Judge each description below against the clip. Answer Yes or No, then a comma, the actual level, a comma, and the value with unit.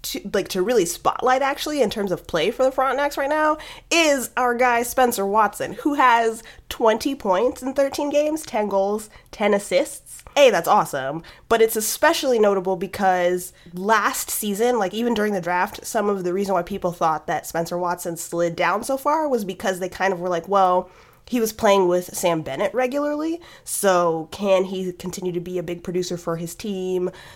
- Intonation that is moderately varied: No, wide, 5.8 semitones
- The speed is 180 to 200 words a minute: Yes, average, 190 wpm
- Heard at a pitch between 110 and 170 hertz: No, high, 205 Hz